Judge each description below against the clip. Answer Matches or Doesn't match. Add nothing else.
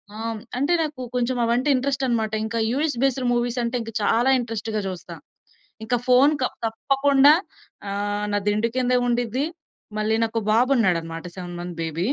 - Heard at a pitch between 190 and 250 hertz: Matches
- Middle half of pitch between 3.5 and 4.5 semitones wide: Matches